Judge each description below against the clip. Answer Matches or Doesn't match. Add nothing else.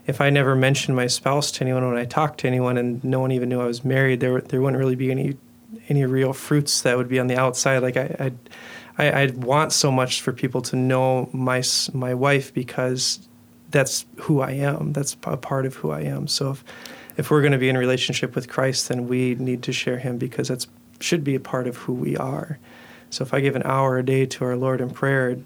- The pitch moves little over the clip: Matches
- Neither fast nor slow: Doesn't match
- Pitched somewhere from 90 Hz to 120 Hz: Doesn't match